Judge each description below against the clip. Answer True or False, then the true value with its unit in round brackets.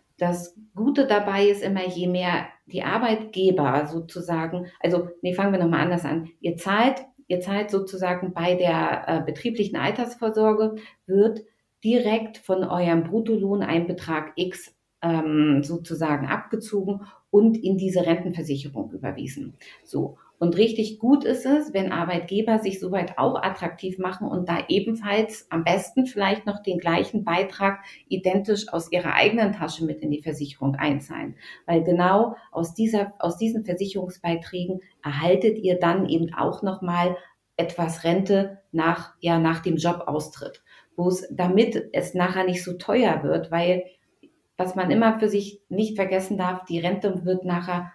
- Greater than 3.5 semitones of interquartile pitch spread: False (3.2 semitones)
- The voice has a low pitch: False (185 Hz)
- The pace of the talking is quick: False (150 wpm)